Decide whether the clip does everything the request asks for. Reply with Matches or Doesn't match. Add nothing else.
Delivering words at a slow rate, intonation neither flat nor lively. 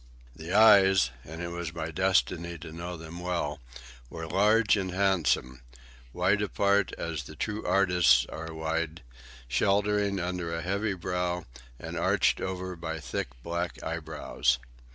Matches